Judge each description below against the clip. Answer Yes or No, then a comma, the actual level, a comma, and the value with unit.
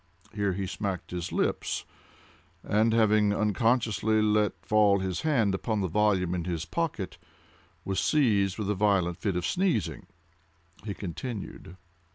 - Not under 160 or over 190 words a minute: No, average, 140 wpm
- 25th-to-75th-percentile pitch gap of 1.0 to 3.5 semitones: Yes, narrow, 2.6 semitones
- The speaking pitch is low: Yes, low, 100 Hz